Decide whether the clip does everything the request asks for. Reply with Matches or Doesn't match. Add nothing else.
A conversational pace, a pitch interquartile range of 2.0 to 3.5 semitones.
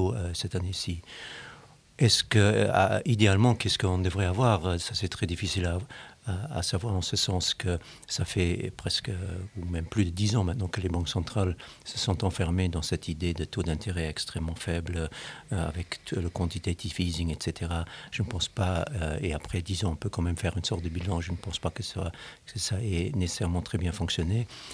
Matches